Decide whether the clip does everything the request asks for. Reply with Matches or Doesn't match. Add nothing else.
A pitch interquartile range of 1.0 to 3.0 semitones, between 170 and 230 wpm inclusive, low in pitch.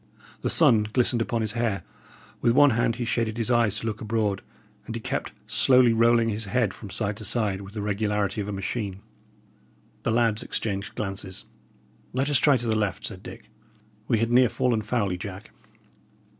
Matches